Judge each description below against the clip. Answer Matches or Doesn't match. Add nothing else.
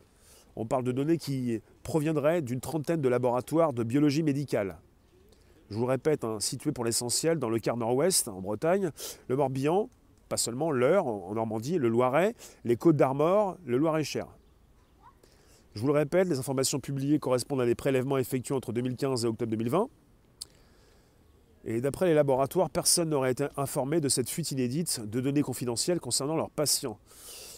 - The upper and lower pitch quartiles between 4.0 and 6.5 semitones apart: Matches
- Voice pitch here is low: Matches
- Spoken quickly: Doesn't match